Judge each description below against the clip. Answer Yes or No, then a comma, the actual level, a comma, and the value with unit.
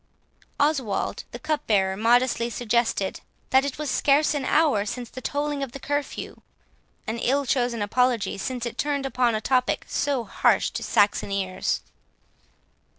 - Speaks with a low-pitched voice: No, very high, 250 Hz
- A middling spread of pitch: Yes, average, 4.0 semitones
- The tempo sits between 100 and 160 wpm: Yes, average, 150 wpm